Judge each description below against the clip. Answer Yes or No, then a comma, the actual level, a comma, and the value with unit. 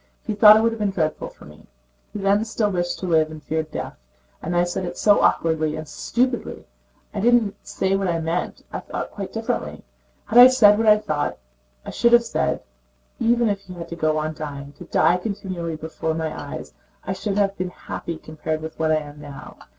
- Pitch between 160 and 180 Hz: Yes, medium, 175 Hz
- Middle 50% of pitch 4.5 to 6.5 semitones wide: Yes, average, 4.9 semitones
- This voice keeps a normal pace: No, fast, 215 wpm